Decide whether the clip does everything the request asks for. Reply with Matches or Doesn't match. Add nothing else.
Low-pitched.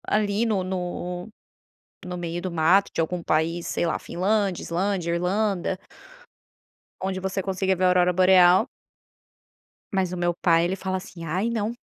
Doesn't match